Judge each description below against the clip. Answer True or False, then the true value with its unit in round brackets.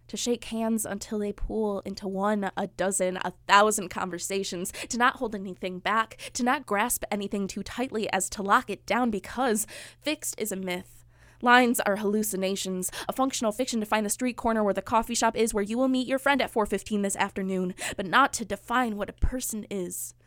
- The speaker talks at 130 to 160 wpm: False (200 wpm)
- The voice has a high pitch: True (205 Hz)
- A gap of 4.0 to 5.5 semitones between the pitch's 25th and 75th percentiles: False (3.3 semitones)